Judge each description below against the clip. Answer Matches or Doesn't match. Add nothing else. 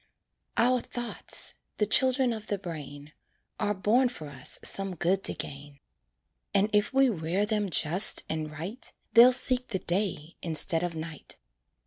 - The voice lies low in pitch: Doesn't match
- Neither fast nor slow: Matches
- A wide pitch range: Matches